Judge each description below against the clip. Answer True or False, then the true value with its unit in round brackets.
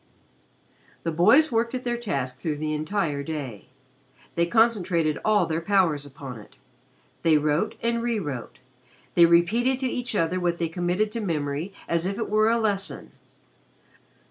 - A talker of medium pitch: True (175 Hz)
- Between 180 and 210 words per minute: False (160 wpm)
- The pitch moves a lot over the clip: True (6.1 semitones)